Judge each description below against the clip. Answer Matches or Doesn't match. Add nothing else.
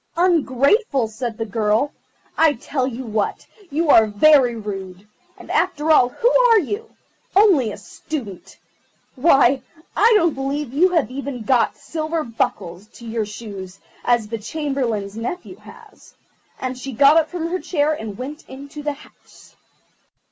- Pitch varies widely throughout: Matches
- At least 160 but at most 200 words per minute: Doesn't match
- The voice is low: Doesn't match